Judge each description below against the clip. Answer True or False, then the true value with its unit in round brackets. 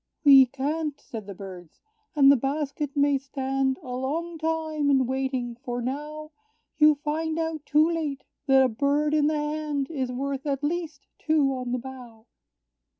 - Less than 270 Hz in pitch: False (280 Hz)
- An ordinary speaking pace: True (165 wpm)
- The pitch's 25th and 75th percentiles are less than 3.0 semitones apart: True (2.5 semitones)